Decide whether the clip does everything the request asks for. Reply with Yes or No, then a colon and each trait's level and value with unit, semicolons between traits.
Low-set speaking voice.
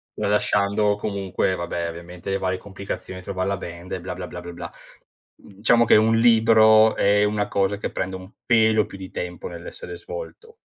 Yes: low, 100 Hz